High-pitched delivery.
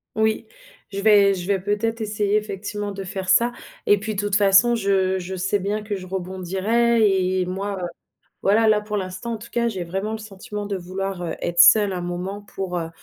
Yes: high, 200 Hz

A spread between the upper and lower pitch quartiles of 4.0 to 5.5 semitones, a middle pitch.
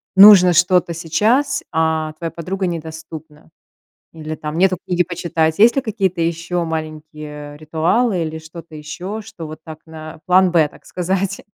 No: narrow, 2.6 semitones; medium, 165 Hz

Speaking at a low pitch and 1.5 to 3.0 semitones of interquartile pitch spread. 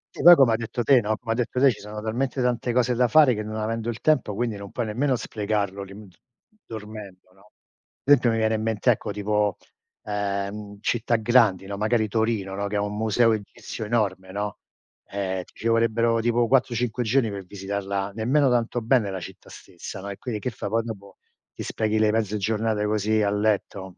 Yes: low, 110 Hz; narrow, 2.6 semitones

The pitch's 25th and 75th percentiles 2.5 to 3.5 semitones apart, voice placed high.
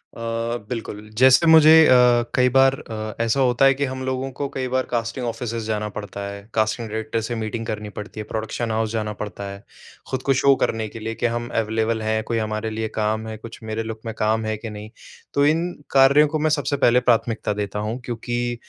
No: average, 2.9 semitones; low, 115 Hz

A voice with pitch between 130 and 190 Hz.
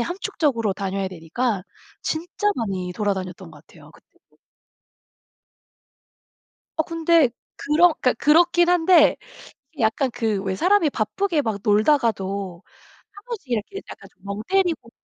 No: high, 245 Hz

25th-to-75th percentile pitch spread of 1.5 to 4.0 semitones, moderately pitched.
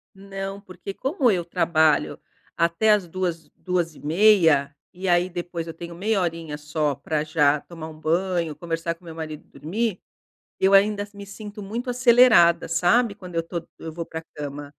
Yes: average, 3.6 semitones; medium, 175 Hz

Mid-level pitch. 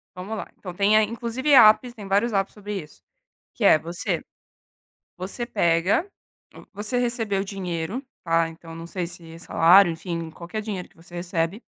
No: high, 195 Hz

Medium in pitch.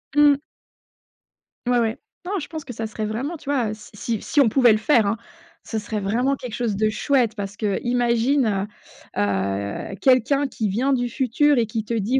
No: high, 230 Hz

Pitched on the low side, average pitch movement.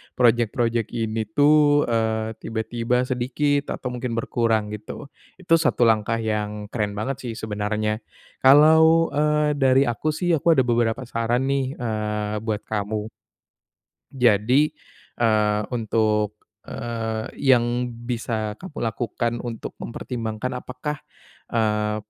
Yes: low, 115 Hz; average, 3.4 semitones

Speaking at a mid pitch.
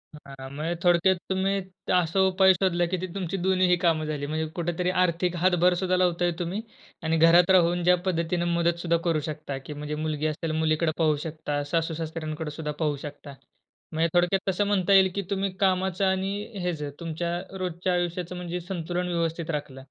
Yes: medium, 170 Hz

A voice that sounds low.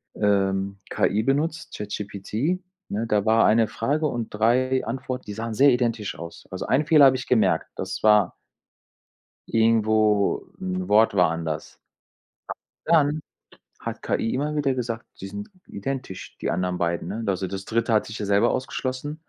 Yes: low, 110 Hz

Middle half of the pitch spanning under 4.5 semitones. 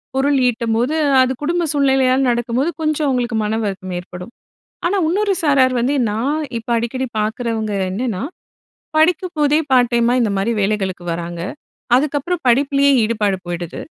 No: average, 4.8 semitones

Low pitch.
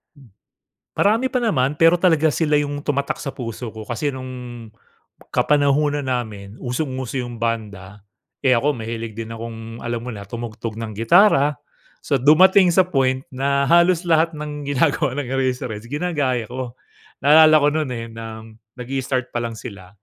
Yes: low, 130 Hz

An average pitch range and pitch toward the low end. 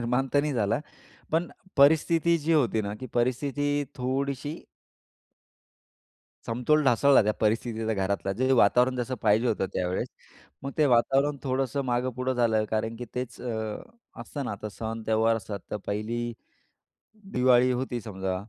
Yes: average, 3.5 semitones; low, 125 Hz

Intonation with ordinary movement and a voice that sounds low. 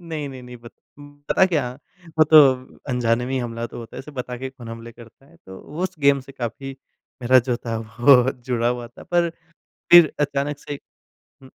Yes: average, 3.3 semitones; low, 130 Hz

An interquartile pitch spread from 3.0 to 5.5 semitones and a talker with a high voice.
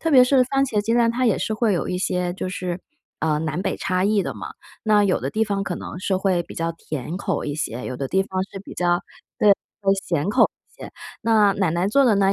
Yes: average, 3.6 semitones; high, 195 Hz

